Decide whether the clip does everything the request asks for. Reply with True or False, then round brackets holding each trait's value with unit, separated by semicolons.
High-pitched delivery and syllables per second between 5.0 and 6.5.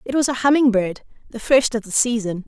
True (235 Hz; 5.7 syllables/s)